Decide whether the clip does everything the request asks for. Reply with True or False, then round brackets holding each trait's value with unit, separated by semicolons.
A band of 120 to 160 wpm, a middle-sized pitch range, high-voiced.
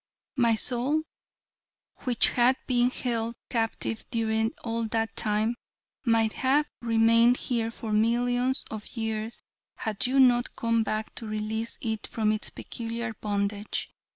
False (135 wpm; 1.7 semitones; 230 Hz)